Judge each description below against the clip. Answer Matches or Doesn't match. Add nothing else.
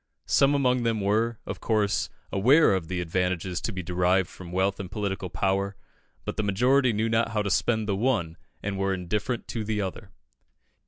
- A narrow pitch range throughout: Doesn't match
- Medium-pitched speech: Doesn't match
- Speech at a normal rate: Matches